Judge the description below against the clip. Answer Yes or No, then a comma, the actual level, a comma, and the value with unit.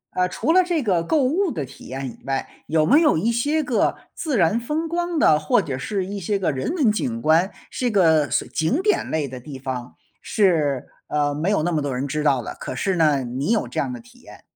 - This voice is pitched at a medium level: Yes, medium, 175 Hz